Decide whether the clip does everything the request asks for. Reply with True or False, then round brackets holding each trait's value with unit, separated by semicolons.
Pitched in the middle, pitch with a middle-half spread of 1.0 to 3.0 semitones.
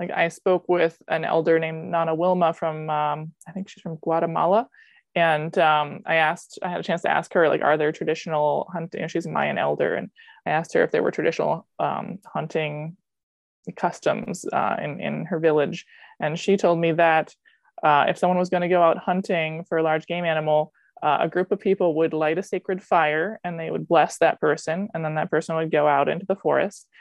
True (165 Hz; 2.6 semitones)